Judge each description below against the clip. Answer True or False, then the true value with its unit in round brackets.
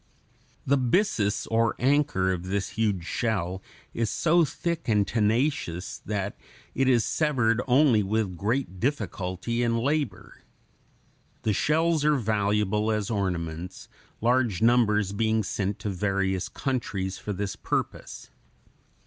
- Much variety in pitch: False (4.3 semitones)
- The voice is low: True (110 Hz)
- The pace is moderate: False (125 wpm)